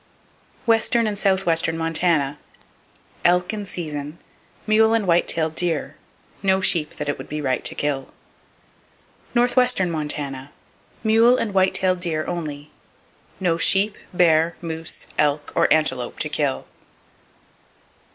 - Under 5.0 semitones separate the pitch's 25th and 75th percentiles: Yes, average, 4.4 semitones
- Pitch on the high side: No, medium, 170 Hz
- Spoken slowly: Yes, slow, 125 wpm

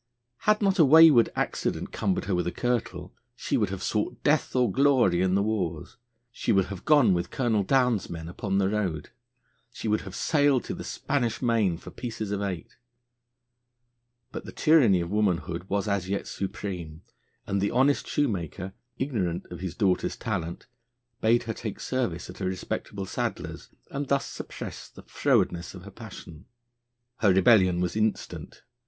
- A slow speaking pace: No, average, 170 wpm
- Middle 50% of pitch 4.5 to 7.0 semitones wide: Yes, average, 4.8 semitones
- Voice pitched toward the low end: Yes, low, 100 Hz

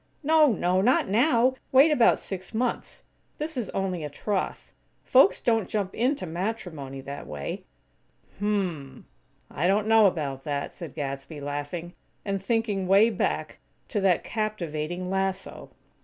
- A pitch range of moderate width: No, wide, 6.0 semitones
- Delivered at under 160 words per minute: Yes, average, 145 wpm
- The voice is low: No, high, 190 Hz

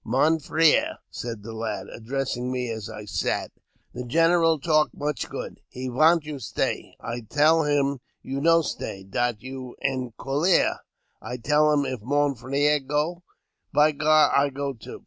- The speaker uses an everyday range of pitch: Yes, average, 3.8 semitones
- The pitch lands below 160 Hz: Yes, medium, 140 Hz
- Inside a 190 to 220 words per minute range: No, average, 170 wpm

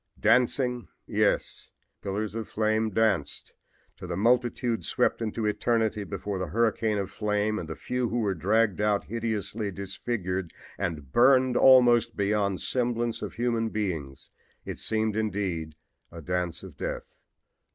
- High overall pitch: No, low, 105 Hz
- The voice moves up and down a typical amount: Yes, average, 3.3 semitones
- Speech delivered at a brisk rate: No, average, 145 wpm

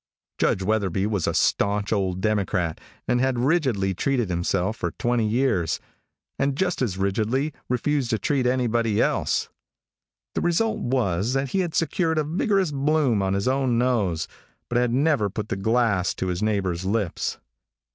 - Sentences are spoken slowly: No, average, 160 wpm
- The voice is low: Yes, low, 115 Hz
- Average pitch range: No, wide, 5.7 semitones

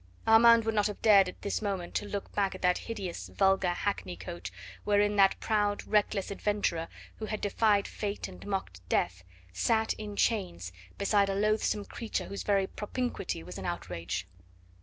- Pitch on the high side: Yes, high, 200 Hz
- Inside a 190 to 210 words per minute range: No, average, 170 wpm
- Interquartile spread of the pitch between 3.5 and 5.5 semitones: No, average, 3.1 semitones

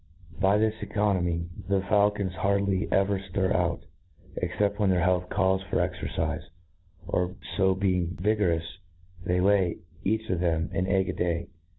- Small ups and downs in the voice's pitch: Yes, narrow, 1.9 semitones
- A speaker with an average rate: Yes, average, 150 wpm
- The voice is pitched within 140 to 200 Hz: No, very low, 95 Hz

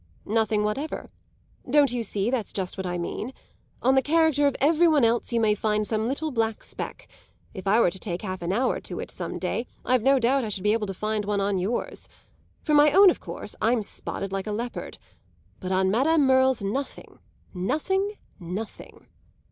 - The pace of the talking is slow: No, average, 200 wpm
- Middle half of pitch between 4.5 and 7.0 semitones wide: Yes, average, 5.2 semitones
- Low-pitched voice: No, high, 225 Hz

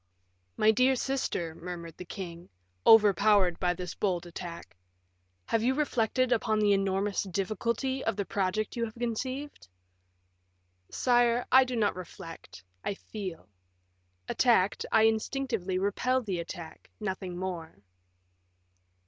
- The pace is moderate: No, slow, 125 wpm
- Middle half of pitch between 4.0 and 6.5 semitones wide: Yes, average, 4.7 semitones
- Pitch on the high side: Yes, high, 205 Hz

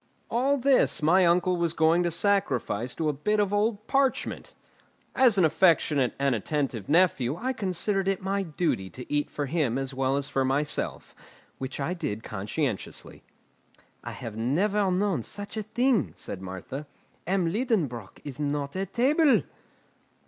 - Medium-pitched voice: Yes, medium, 165 Hz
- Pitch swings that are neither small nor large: No, wide, 6.9 semitones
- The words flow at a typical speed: Yes, average, 155 wpm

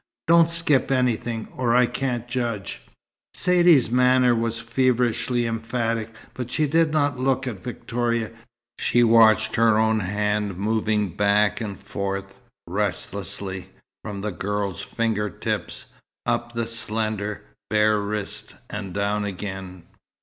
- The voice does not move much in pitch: No, average, 3.1 semitones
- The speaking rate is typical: No, slow, 125 wpm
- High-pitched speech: No, low, 110 Hz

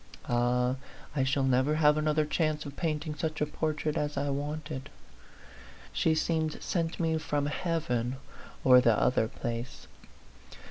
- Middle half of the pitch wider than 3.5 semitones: No, average, 3.0 semitones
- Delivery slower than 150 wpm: Yes, average, 140 wpm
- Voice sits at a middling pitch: Yes, medium, 150 Hz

